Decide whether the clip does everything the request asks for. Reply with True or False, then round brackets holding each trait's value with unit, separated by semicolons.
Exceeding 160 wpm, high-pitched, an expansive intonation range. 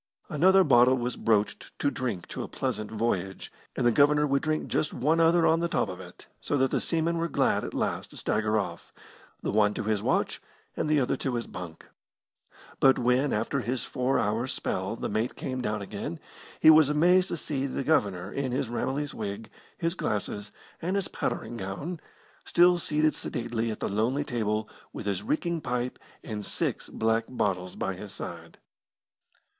False (185 wpm; 125 Hz; 5.9 semitones)